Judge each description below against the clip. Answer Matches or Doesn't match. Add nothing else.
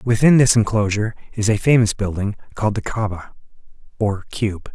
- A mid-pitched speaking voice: Doesn't match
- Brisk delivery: Doesn't match